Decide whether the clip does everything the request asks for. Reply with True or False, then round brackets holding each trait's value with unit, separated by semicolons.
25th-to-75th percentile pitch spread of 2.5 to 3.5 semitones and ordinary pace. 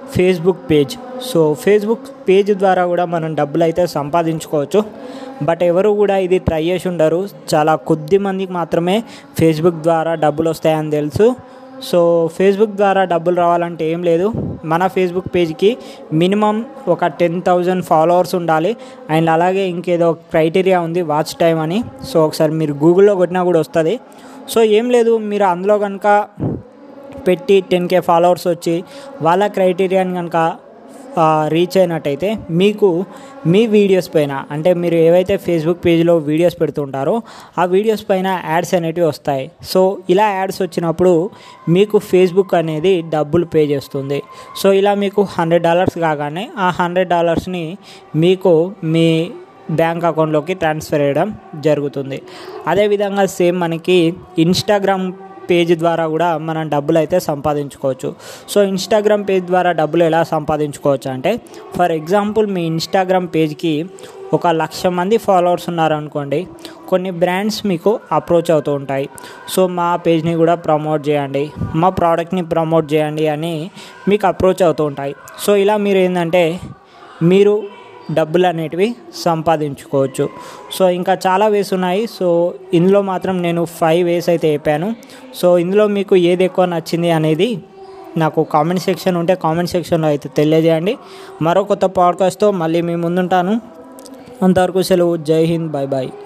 False (3.0 semitones; 135 wpm)